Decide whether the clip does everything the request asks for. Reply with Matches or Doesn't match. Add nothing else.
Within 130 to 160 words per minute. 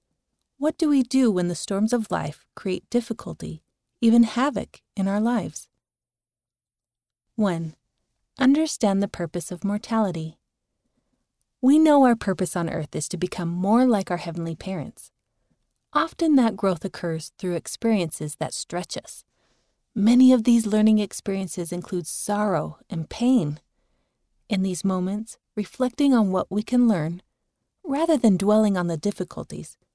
Matches